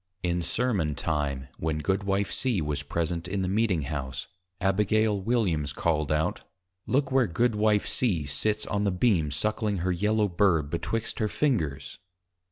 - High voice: No, very low, 95 Hz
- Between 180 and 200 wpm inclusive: No, average, 155 wpm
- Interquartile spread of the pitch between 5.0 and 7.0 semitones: Yes, wide, 5.5 semitones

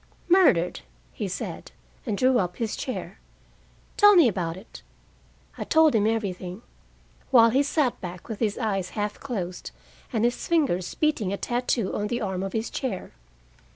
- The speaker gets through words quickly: No, average, 160 wpm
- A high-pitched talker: Yes, high, 220 Hz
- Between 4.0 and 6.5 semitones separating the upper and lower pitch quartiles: Yes, average, 5.1 semitones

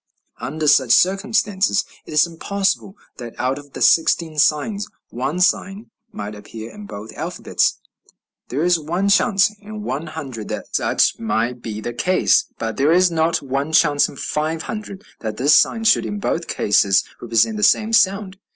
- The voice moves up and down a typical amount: No, wide, 7.5 semitones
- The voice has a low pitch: No, medium, 160 Hz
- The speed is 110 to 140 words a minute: No, average, 170 wpm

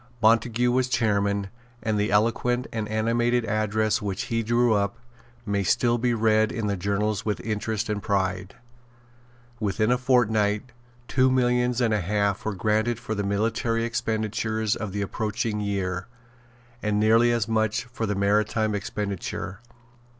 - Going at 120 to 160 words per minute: Yes, average, 150 wpm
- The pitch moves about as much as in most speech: No, narrow, 2.2 semitones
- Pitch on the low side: Yes, low, 110 Hz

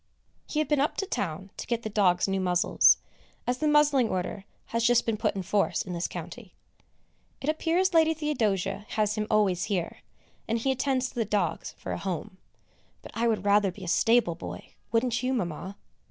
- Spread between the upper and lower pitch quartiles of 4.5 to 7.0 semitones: Yes, average, 5.0 semitones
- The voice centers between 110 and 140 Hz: No, high, 215 Hz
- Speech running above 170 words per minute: Yes, average, 195 wpm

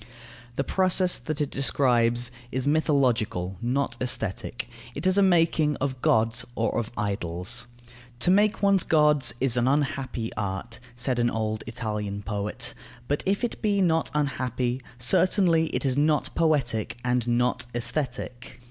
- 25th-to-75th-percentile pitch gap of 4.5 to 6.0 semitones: Yes, average, 4.8 semitones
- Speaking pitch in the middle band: No, low, 125 Hz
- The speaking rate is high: No, average, 145 wpm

